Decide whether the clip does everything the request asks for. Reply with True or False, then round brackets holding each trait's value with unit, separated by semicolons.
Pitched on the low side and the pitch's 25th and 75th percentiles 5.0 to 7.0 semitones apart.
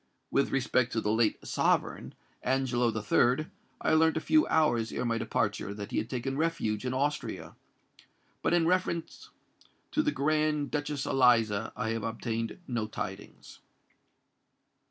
True (125 Hz; 5.3 semitones)